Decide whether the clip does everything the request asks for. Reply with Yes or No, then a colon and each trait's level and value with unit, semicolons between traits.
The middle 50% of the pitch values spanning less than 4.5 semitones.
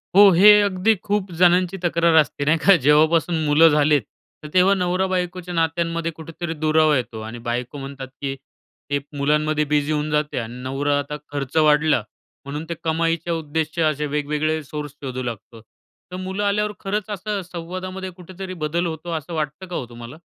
Yes: average, 3.5 semitones